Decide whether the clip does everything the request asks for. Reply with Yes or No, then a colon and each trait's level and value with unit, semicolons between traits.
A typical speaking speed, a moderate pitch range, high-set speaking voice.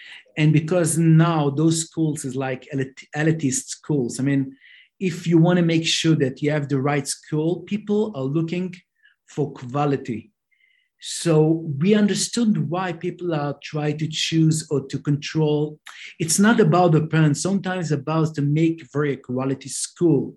No: average, 155 wpm; average, 3.6 semitones; medium, 155 Hz